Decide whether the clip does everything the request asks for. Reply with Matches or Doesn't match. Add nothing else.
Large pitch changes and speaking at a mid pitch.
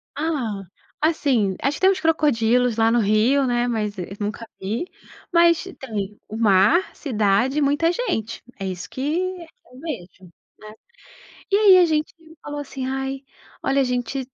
Doesn't match